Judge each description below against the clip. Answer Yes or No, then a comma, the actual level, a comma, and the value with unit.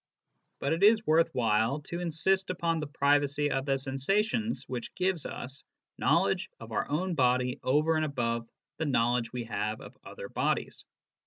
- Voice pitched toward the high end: No, medium, 145 Hz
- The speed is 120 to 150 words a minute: No, average, 165 wpm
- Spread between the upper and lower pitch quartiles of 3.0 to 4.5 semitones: No, average, 4.9 semitones